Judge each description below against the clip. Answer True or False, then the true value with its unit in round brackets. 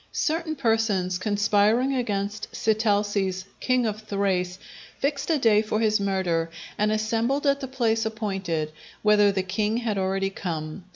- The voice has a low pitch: False (210 Hz)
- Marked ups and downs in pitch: False (2.8 semitones)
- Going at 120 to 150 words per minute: True (140 wpm)